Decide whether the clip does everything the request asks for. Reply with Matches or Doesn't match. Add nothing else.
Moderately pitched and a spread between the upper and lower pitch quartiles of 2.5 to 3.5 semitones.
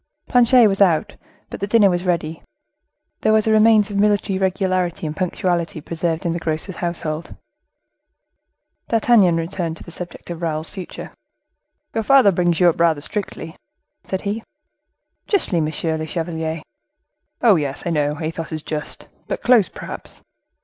Doesn't match